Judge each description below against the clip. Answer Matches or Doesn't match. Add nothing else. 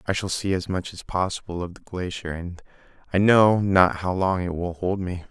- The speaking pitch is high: Doesn't match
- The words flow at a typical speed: Doesn't match